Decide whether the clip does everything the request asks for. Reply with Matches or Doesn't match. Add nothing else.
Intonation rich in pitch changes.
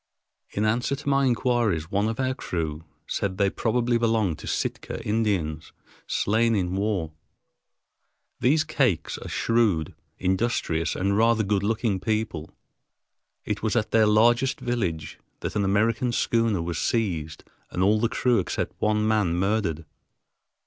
Doesn't match